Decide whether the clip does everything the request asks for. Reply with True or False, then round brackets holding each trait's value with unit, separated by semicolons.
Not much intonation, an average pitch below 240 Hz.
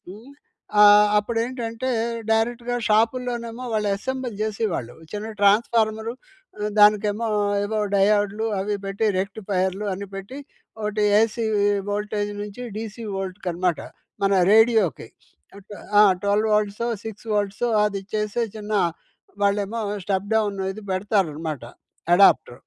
True (2.0 semitones; 210 Hz)